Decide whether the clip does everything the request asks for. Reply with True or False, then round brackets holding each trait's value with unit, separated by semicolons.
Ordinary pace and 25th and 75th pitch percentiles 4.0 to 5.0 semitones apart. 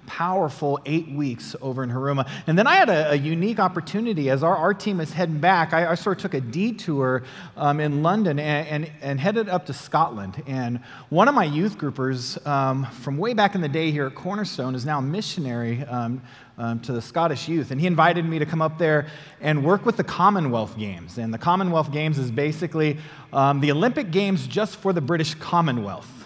False (215 wpm; 4.7 semitones)